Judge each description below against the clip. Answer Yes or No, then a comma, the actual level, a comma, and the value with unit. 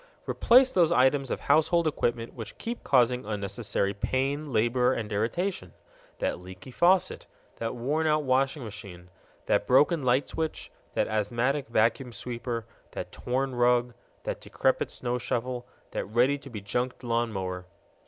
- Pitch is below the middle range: Yes, low, 125 Hz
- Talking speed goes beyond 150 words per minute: No, average, 145 wpm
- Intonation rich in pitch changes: No, average, 3.7 semitones